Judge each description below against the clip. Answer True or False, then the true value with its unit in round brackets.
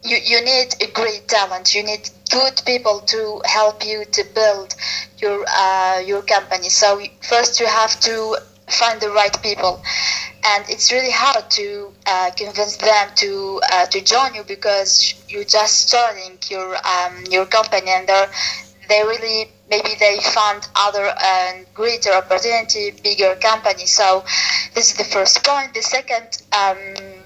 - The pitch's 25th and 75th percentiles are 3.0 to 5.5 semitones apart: False (2.6 semitones)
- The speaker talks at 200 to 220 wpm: False (155 wpm)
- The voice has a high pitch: True (210 Hz)